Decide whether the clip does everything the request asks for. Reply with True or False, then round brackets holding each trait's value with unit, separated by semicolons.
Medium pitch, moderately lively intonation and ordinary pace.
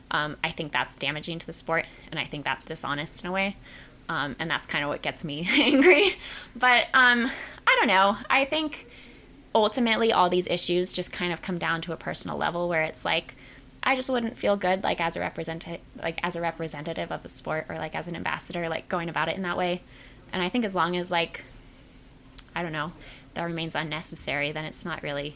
False (170 Hz; 3.9 semitones; 220 wpm)